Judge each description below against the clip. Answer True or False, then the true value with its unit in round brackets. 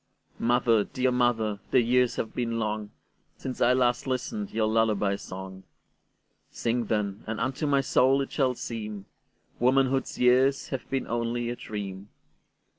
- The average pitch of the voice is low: True (120 Hz)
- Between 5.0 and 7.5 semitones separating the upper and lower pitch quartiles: False (3.1 semitones)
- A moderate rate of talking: False (130 wpm)